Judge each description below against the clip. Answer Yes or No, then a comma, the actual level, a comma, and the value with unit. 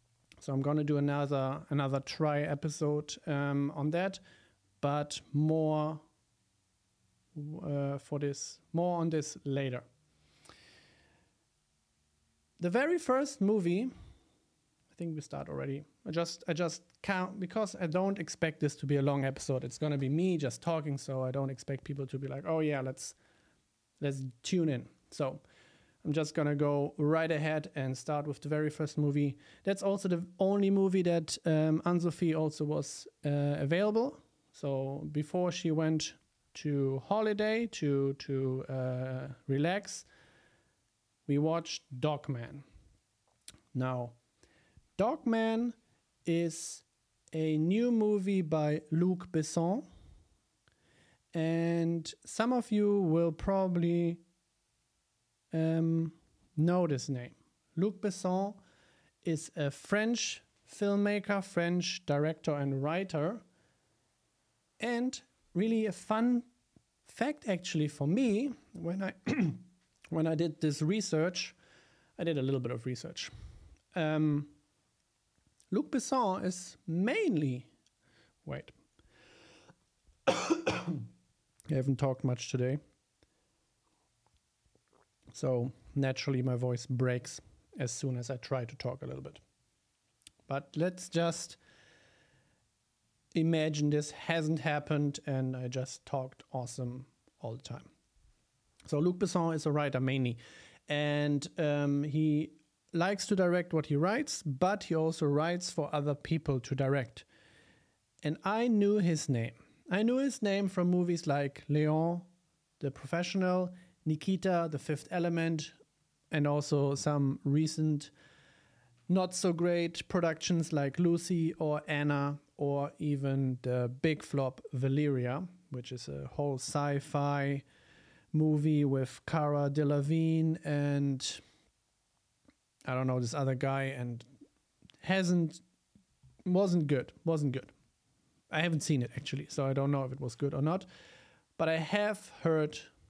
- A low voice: No, medium, 150 Hz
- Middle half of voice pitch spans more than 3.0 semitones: Yes, average, 4.0 semitones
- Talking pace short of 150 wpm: Yes, slow, 125 wpm